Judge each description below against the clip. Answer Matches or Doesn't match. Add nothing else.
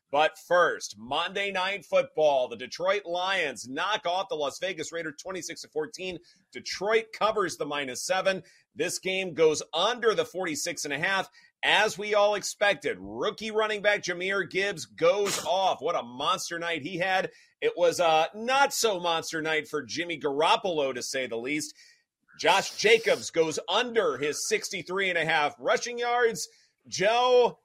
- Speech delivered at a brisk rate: Doesn't match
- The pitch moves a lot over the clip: Matches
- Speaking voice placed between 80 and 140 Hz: Doesn't match